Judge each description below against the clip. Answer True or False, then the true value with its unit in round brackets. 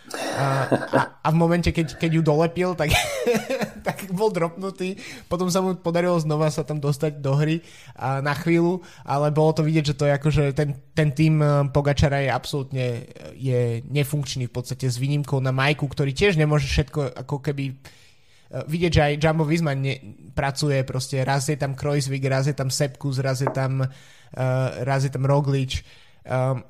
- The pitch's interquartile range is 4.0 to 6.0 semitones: False (2.8 semitones)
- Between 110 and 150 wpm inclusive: False (165 wpm)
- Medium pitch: True (145 Hz)